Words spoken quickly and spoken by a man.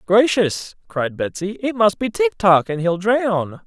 No: average, 180 wpm; male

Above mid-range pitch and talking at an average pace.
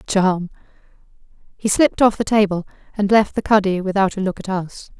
Yes: high, 200 Hz; average, 180 wpm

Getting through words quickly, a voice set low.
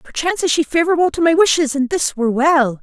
No: fast, 235 wpm; very high, 300 Hz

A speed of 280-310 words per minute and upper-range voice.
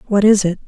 No: fast, 270 wpm; high, 200 Hz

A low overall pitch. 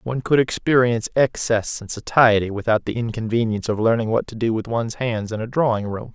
Yes: low, 115 Hz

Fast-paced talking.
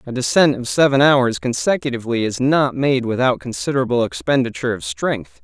No: average, 155 wpm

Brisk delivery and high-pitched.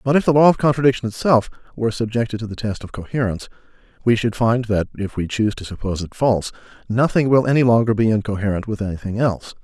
No: fast, 210 wpm; low, 115 Hz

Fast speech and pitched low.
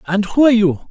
No: fast, 265 wpm; high, 205 Hz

